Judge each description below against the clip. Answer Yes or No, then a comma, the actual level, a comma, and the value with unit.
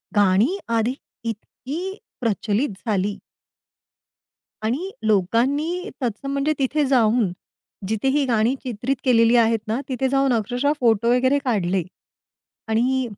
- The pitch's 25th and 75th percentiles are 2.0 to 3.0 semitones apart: No, average, 3.8 semitones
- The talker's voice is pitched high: Yes, high, 245 Hz